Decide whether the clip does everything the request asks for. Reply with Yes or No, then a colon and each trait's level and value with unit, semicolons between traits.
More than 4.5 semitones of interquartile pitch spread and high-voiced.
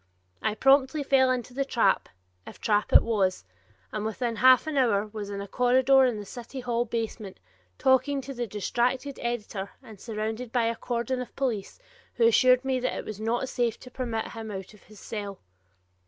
No: average, 3.2 semitones; high, 235 Hz